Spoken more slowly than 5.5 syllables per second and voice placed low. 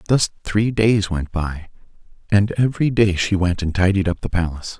Yes: 5.2 syllables/s; very low, 95 Hz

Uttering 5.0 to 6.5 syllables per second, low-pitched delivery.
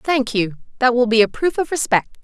No: 5.4 syllables/s; very high, 250 Hz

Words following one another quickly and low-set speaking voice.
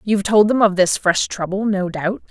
No: fast, 235 wpm; high, 195 Hz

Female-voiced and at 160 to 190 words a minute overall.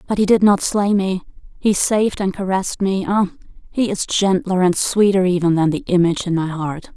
No: female; fast, 205 wpm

